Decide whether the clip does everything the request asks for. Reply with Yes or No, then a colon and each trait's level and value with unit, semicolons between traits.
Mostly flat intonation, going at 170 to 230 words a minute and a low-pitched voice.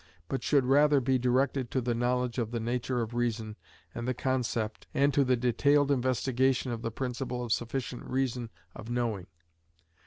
Yes: narrow, 2.0 semitones; average, 175 wpm; low, 125 Hz